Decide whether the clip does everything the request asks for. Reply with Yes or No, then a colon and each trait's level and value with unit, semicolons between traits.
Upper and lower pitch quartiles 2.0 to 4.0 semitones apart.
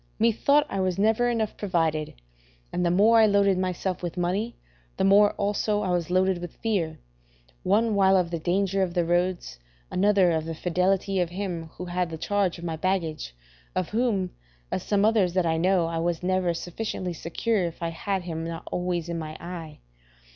Yes: average, 2.8 semitones